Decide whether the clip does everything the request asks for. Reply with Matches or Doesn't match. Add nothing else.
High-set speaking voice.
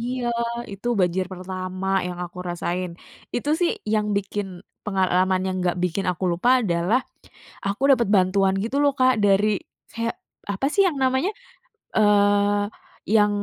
Matches